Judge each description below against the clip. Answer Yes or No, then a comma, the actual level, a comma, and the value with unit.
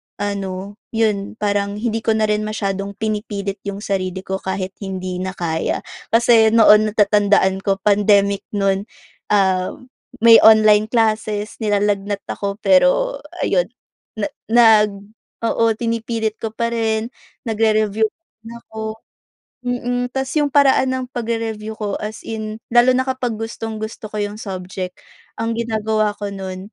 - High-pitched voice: Yes, high, 215 Hz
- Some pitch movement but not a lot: No, narrow, 2.2 semitones